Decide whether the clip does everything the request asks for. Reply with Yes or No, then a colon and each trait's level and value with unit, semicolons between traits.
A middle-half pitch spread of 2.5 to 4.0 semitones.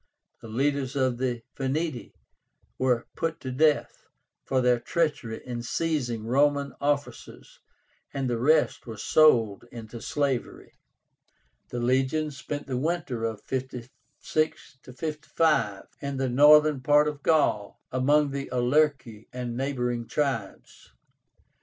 Yes: average, 3.4 semitones